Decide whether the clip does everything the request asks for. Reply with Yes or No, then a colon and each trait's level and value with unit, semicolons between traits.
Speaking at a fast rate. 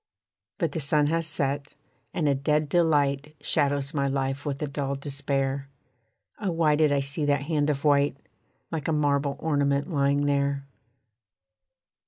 No: average, 155 wpm